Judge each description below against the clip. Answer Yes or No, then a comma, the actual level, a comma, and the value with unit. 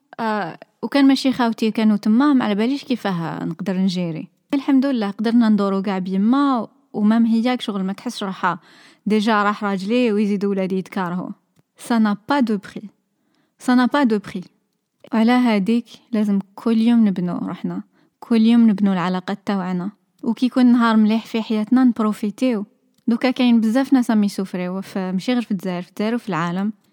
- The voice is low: No, high, 215 Hz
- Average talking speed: No, fast, 150 wpm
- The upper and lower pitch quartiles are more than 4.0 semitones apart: No, average, 3.4 semitones